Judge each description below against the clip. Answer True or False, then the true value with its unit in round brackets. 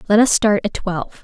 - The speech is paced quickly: True (245 wpm)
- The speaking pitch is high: True (200 Hz)